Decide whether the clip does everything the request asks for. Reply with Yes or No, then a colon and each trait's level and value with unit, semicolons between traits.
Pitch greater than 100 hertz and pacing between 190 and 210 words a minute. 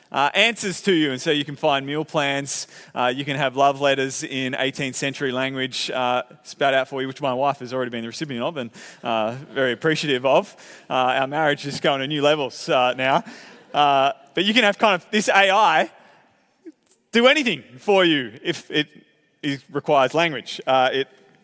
Yes: medium, 140 Hz; average, 200 wpm